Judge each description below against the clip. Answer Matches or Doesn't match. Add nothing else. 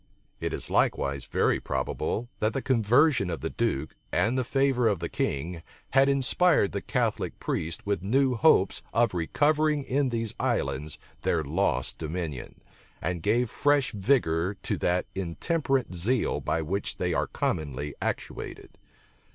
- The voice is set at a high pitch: Doesn't match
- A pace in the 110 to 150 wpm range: Matches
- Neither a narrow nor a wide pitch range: Doesn't match